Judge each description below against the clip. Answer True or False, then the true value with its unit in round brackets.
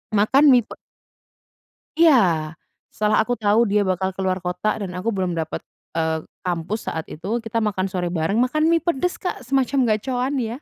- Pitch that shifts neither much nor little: False (5.9 semitones)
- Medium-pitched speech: False (210 Hz)